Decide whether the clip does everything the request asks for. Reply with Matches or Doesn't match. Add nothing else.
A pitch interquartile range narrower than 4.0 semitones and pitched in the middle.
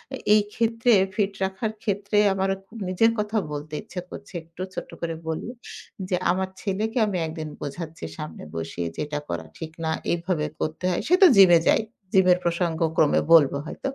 Doesn't match